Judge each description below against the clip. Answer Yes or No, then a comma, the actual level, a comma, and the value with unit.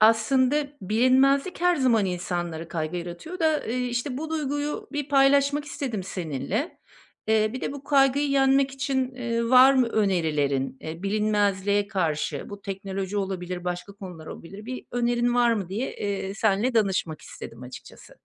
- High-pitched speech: Yes, high, 220 Hz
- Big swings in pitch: Yes, wide, 6.1 semitones